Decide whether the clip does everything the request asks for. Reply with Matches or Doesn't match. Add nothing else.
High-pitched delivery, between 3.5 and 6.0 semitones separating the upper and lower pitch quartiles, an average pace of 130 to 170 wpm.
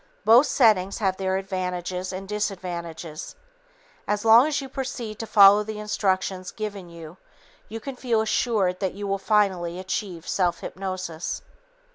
Doesn't match